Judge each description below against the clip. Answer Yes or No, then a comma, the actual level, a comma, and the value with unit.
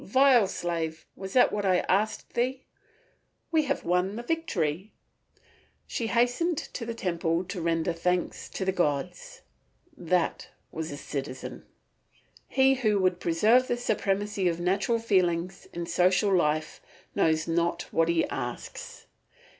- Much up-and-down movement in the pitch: No, average, 5.0 semitones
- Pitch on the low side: No, medium, 185 Hz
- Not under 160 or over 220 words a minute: No, average, 140 wpm